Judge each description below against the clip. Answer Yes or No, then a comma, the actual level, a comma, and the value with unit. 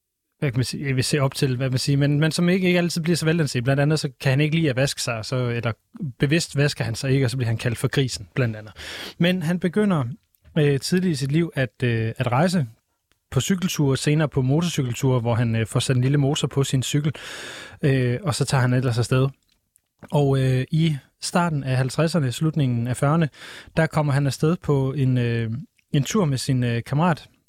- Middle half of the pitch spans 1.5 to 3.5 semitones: No, average, 3.9 semitones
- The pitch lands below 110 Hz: No, medium, 140 Hz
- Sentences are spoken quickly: Yes, fast, 230 wpm